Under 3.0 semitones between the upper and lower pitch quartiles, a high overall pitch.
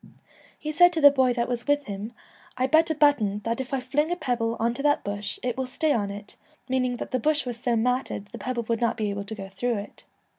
No: average, 4.3 semitones; high, 245 Hz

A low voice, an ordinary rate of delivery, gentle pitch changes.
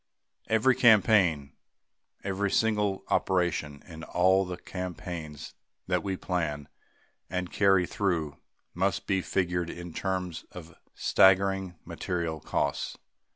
No: very low, 90 Hz; slow, 110 wpm; narrow, 2.2 semitones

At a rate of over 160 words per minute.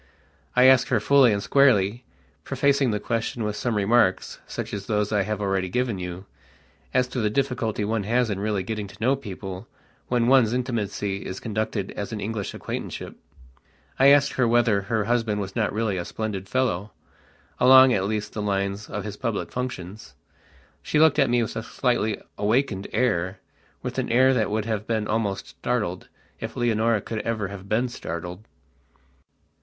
Yes: average, 170 wpm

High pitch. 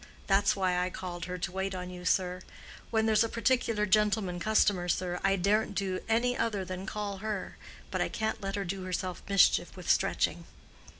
Yes: high, 195 Hz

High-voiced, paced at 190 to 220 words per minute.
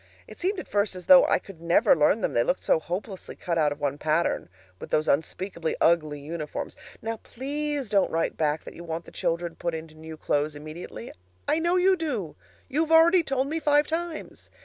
No: medium, 175 Hz; fast, 205 wpm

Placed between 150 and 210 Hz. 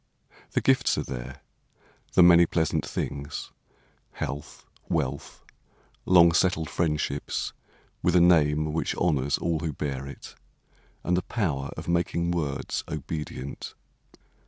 No: very low, 80 Hz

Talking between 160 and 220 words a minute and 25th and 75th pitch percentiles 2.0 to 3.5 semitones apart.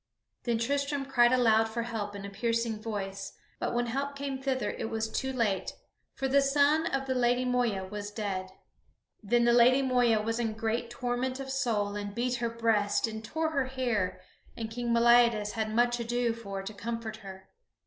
Yes: average, 190 wpm; average, 2.8 semitones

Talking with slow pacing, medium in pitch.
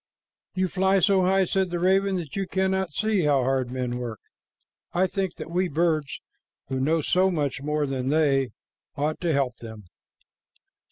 No: average, 170 wpm; medium, 160 Hz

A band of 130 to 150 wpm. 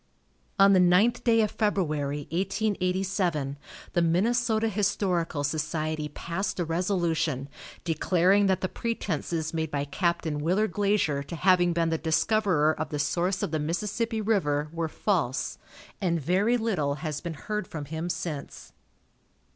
Yes: average, 140 wpm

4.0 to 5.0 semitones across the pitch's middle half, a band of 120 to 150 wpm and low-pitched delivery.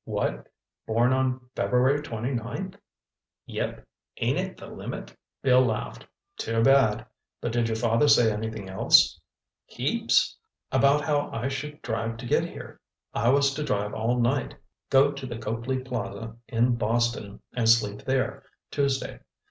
No: average, 3.0 semitones; average, 145 wpm; low, 120 Hz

